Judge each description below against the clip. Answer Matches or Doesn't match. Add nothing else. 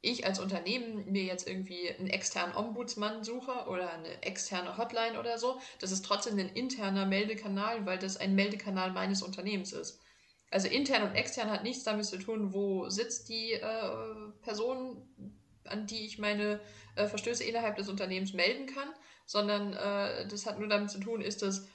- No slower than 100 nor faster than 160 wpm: Doesn't match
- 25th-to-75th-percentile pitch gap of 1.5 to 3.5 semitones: Matches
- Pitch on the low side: Doesn't match